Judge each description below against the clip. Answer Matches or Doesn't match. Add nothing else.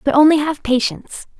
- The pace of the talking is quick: Doesn't match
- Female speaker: Matches